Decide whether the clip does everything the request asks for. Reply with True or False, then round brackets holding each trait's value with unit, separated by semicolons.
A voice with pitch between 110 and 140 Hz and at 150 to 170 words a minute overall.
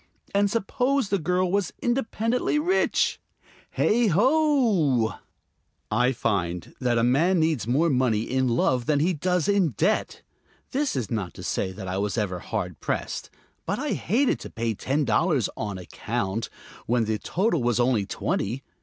True (135 Hz; 165 wpm)